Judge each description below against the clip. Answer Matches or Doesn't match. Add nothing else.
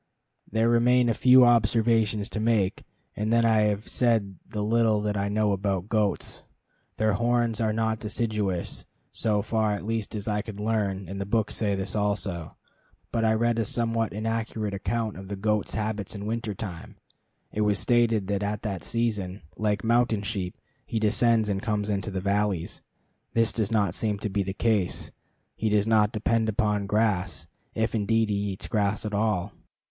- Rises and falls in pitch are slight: Matches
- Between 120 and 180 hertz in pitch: Doesn't match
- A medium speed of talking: Matches